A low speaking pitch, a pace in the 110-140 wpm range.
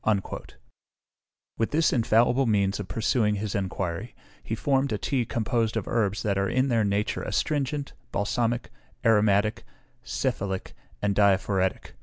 Yes: low, 110 Hz; slow, 135 wpm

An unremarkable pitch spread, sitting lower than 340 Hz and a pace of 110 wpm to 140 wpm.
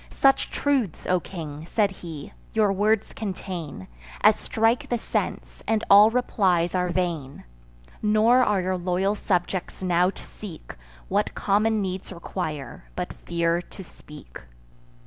Yes: average, 3.7 semitones; medium, 185 Hz; slow, 135 wpm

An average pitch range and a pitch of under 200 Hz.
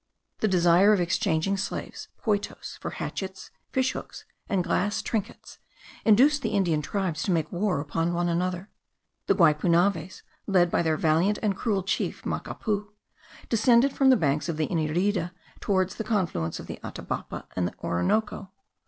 Yes: average, 3.8 semitones; medium, 185 Hz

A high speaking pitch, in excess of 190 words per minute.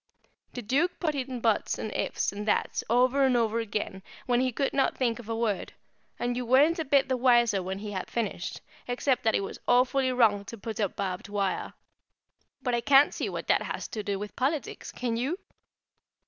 Yes: high, 240 Hz; fast, 205 wpm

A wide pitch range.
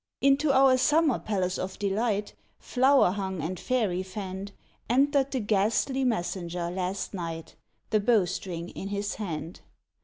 Yes: wide, 5.7 semitones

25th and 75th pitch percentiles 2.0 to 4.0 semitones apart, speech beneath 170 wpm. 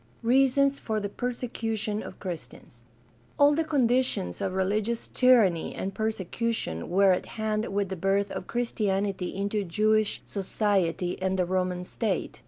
Yes: average, 3.6 semitones; average, 150 wpm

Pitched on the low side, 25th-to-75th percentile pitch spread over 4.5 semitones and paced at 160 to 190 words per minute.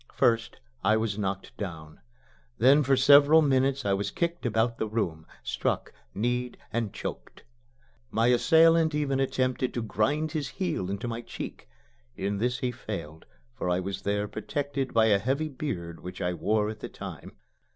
Yes: low, 115 Hz; average, 5.3 semitones; average, 165 wpm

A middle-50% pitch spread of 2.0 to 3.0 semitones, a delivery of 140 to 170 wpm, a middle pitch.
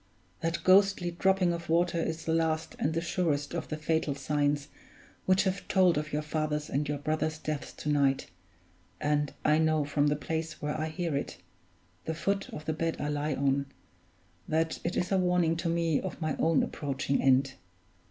No: narrow, 2.4 semitones; average, 190 wpm; medium, 155 Hz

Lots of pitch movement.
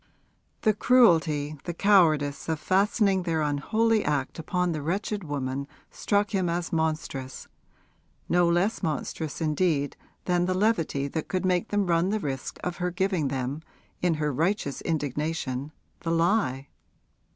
No: average, 4.3 semitones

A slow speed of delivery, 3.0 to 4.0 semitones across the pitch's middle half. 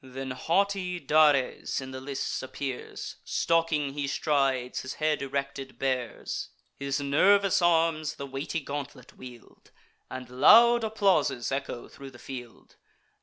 Yes: slow, 125 wpm; average, 3.7 semitones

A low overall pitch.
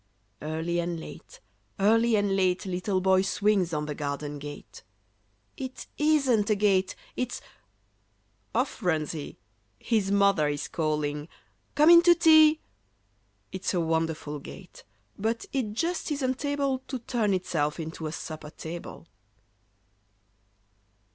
No: high, 190 Hz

